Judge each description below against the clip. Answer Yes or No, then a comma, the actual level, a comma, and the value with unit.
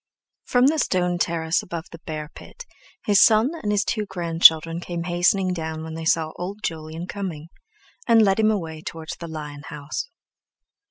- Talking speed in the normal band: Yes, average, 170 wpm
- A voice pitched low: No, medium, 170 Hz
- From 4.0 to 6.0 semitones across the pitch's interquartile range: No, average, 3.6 semitones